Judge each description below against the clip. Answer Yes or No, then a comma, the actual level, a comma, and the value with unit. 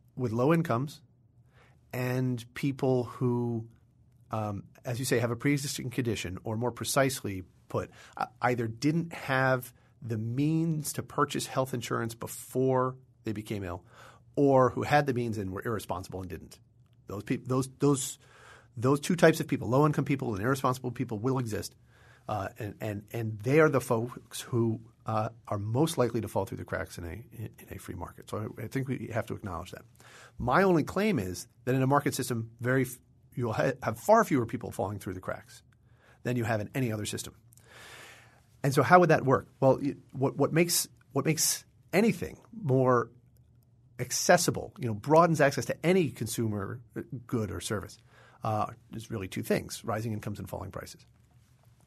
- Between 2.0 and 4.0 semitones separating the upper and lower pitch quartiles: Yes, average, 2.7 semitones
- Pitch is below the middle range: Yes, low, 120 Hz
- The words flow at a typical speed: Yes, average, 180 wpm